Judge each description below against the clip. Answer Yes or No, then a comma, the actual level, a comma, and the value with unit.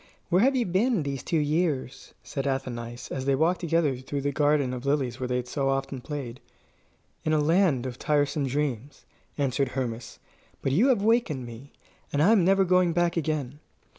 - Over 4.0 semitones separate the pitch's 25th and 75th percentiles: Yes, average, 4.4 semitones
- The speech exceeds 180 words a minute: Yes, average, 190 wpm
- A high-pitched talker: No, medium, 145 Hz